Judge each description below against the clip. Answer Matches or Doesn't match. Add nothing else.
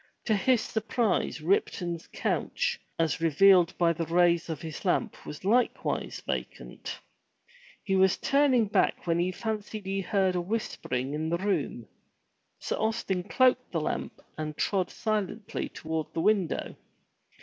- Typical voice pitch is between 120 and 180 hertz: Doesn't match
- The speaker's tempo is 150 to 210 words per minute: Doesn't match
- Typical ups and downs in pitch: Matches